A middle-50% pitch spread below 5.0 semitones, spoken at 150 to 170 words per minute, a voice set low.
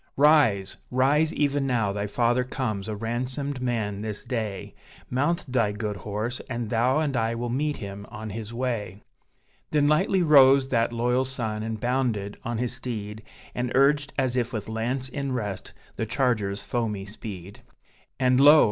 Yes: average, 3.7 semitones; average, 165 wpm; low, 120 Hz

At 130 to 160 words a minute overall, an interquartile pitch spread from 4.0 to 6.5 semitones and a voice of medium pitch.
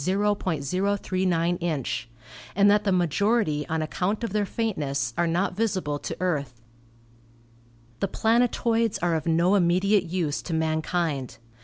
Yes: slow, 135 wpm; average, 4.3 semitones; medium, 180 Hz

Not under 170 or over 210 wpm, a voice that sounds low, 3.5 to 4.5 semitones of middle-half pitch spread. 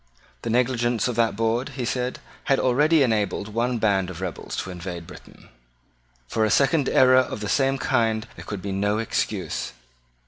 Yes: average, 175 wpm; low, 115 Hz; average, 3.9 semitones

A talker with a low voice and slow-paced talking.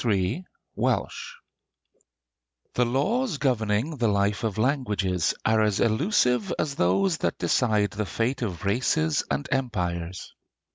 Yes: low, 115 Hz; slow, 125 wpm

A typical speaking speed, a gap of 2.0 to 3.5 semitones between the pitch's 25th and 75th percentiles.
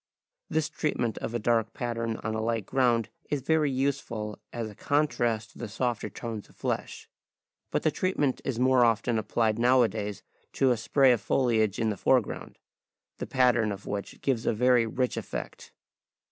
Yes: average, 175 wpm; average, 2.7 semitones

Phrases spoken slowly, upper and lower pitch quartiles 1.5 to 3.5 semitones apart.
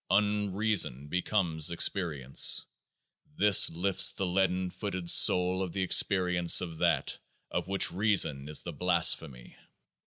Yes: slow, 125 wpm; average, 2.8 semitones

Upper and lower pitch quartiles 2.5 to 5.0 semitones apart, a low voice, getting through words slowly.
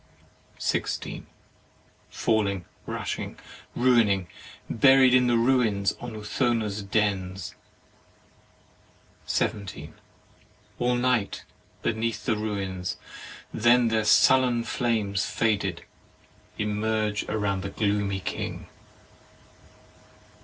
Yes: average, 3.0 semitones; low, 110 Hz; slow, 80 wpm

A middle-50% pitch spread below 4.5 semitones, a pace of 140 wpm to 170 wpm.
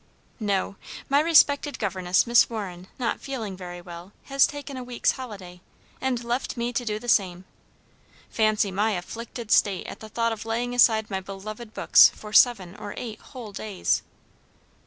Yes: average, 3.9 semitones; average, 165 wpm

